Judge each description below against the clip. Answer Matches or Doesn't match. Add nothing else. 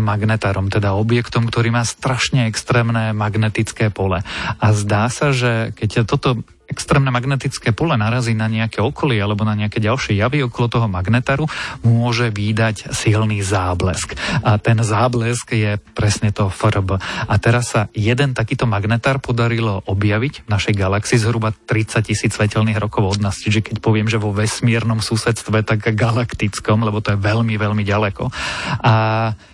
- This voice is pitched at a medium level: Doesn't match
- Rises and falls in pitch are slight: Matches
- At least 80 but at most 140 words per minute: Doesn't match